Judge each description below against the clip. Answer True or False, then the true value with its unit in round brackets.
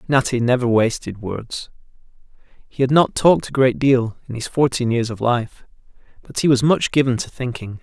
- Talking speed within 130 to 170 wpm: False (185 wpm)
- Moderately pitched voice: False (125 Hz)